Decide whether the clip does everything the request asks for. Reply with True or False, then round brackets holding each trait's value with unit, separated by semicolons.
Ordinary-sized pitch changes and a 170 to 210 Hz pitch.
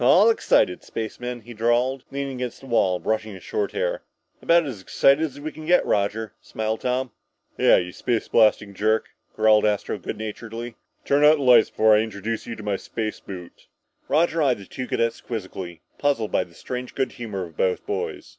False (4.1 semitones; 115 Hz)